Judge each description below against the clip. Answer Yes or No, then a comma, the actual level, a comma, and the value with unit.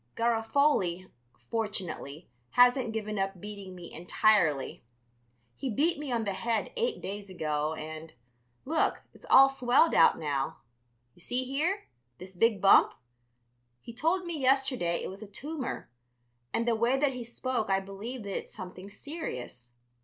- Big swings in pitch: Yes, wide, 6.1 semitones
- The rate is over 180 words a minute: No, average, 150 wpm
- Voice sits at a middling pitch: No, high, 220 Hz